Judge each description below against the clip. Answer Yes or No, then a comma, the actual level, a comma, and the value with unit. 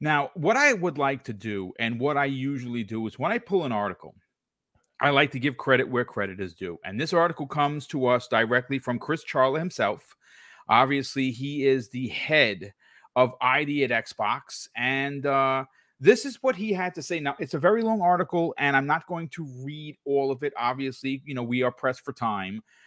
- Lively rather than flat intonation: No, average, 3.4 semitones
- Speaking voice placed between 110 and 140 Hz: Yes, low, 135 Hz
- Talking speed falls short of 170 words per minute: No, fast, 205 wpm